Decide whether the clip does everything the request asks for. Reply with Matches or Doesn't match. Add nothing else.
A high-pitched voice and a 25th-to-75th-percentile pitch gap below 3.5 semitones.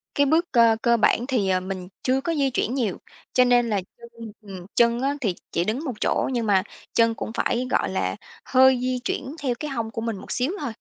Matches